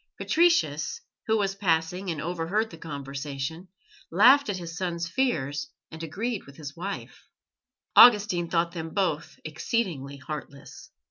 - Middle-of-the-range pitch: Yes, medium, 170 Hz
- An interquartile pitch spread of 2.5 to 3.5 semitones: No, average, 4.7 semitones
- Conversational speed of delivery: No, slow, 130 wpm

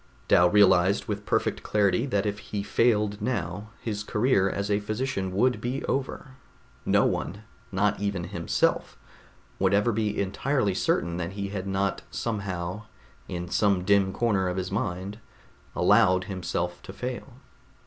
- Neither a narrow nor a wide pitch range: No, narrow, 2.3 semitones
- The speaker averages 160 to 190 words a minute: No, average, 150 wpm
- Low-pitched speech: Yes, low, 100 Hz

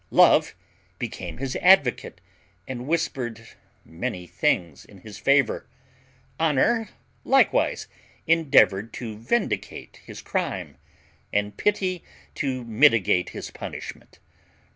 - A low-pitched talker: Yes, low, 125 Hz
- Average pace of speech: No, slow, 100 wpm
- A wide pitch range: Yes, wide, 7.5 semitones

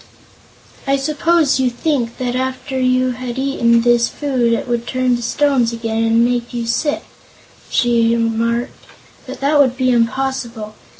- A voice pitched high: Yes, high, 245 Hz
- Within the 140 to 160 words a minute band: Yes, average, 155 wpm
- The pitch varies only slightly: Yes, narrow, 2.2 semitones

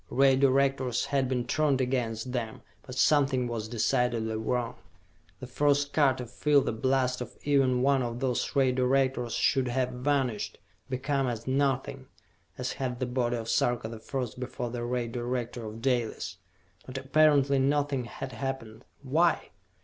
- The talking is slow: No, average, 155 wpm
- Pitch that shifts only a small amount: Yes, narrow, 2.1 semitones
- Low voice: Yes, low, 130 Hz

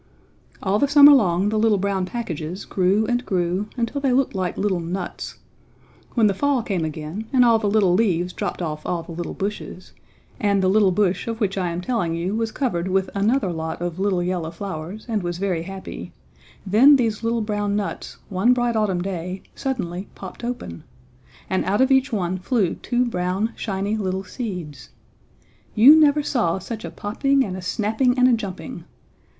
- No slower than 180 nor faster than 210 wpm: Yes, average, 185 wpm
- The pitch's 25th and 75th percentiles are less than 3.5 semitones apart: No, average, 4.3 semitones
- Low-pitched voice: No, high, 200 Hz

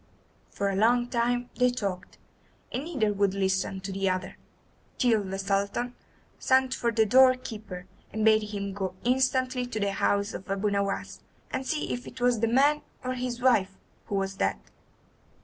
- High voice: Yes, high, 220 Hz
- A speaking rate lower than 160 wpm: No, average, 175 wpm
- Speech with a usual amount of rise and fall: Yes, average, 4.1 semitones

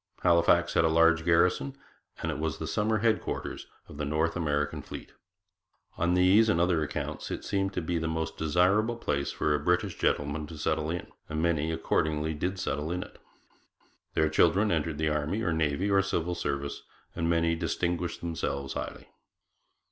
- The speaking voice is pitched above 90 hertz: No, very low, 85 Hz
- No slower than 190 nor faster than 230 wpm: No, average, 175 wpm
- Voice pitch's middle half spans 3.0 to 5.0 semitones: No, narrow, 2.5 semitones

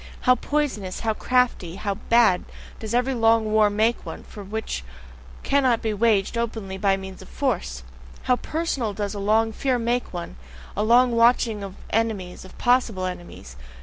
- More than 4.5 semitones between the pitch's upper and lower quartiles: No, average, 3.6 semitones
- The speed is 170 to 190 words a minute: No, average, 160 wpm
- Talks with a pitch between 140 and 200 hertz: No, high, 220 Hz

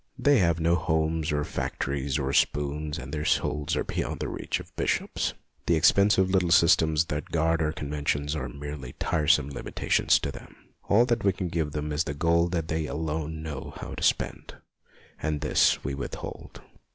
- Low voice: Yes, very low, 80 Hz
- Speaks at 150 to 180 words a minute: No, average, 190 wpm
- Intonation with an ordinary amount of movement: No, narrow, 2.3 semitones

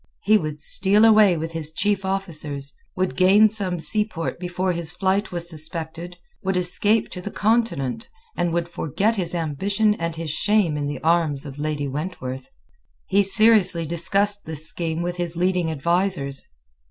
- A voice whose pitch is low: No, medium, 175 Hz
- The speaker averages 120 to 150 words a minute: No, average, 160 wpm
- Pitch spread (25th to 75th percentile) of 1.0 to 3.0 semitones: No, average, 3.7 semitones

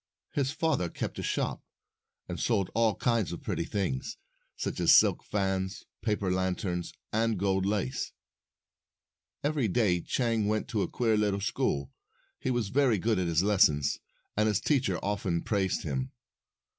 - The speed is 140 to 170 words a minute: Yes, average, 155 wpm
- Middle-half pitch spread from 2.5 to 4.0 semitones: Yes, average, 3.7 semitones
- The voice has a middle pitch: No, low, 100 Hz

